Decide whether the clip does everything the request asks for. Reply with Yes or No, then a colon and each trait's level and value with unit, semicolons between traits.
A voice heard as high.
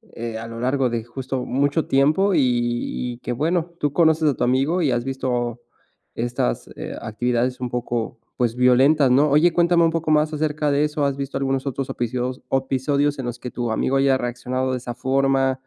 No: low, 130 Hz